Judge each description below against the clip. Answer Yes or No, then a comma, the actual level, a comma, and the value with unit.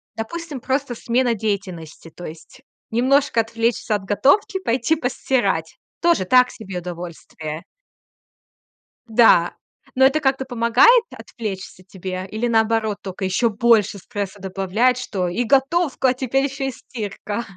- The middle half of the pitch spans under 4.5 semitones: No, average, 5.2 semitones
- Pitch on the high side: Yes, high, 230 Hz